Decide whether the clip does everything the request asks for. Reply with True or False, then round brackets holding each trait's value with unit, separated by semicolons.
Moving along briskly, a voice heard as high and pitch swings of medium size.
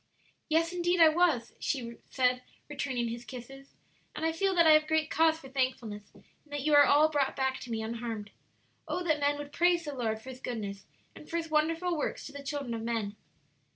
True (215 wpm; 285 Hz; 4.9 semitones)